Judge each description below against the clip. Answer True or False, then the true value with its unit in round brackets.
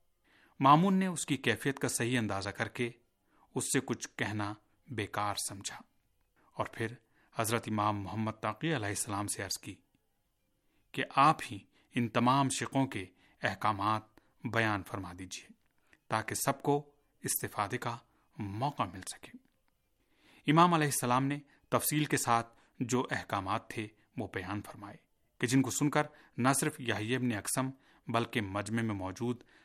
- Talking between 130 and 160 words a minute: True (145 wpm)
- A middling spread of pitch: True (4.7 semitones)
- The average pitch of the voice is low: True (120 Hz)